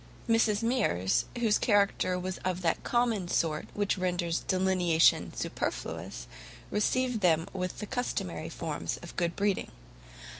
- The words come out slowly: Yes, slow, 125 wpm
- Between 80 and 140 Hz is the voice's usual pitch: No, medium, 185 Hz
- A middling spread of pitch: Yes, average, 3.5 semitones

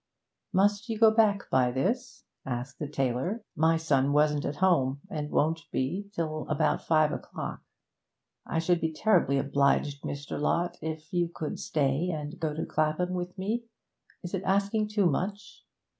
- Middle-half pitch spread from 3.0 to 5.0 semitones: Yes, average, 4.6 semitones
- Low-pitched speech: No, medium, 160 Hz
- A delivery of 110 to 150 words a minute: No, average, 160 wpm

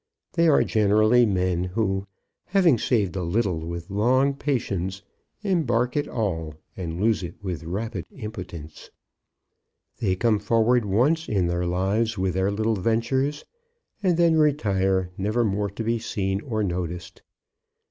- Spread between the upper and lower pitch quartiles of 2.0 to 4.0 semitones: No, average, 4.5 semitones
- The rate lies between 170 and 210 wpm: No, average, 140 wpm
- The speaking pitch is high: No, low, 105 Hz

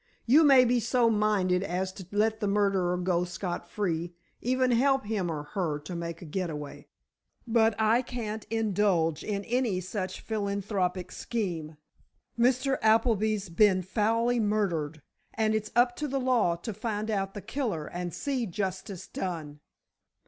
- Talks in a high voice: Yes, high, 205 Hz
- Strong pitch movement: No, average, 4.1 semitones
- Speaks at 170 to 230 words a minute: No, average, 150 wpm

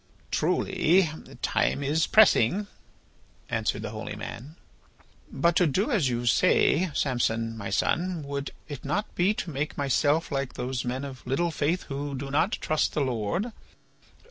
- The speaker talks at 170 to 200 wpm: No, average, 150 wpm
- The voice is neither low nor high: Yes, medium, 145 Hz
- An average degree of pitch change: Yes, average, 4.7 semitones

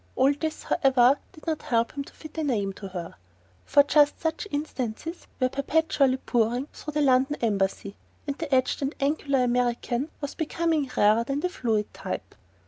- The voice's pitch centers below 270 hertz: No, very high, 275 Hz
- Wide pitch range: No, average, 3.8 semitones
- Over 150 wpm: Yes, average, 175 wpm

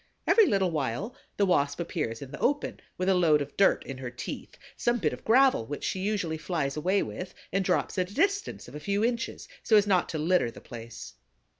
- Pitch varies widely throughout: Yes, wide, 6.0 semitones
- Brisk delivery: Yes, fast, 225 wpm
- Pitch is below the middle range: No, medium, 180 Hz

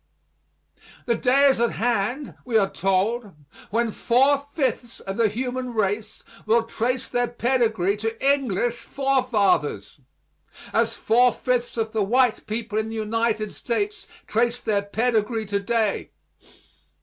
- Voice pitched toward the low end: No, high, 230 Hz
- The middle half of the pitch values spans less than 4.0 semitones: Yes, narrow, 2.6 semitones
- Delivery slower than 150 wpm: Yes, slow, 135 wpm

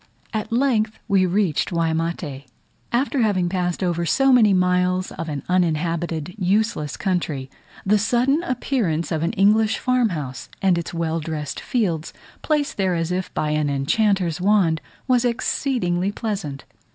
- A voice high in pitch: No, medium, 180 Hz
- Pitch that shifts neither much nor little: Yes, average, 4.8 semitones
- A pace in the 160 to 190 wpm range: No, average, 145 wpm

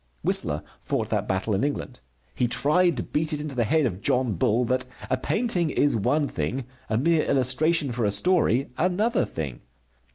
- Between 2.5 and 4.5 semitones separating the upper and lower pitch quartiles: No, wide, 5.6 semitones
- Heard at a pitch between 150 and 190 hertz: No, low, 130 Hz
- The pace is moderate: Yes, average, 185 wpm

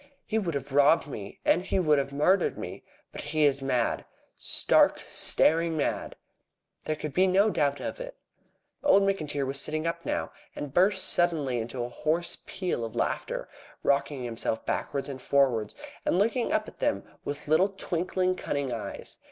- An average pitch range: Yes, average, 5.0 semitones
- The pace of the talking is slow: No, average, 170 wpm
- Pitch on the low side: No, medium, 155 Hz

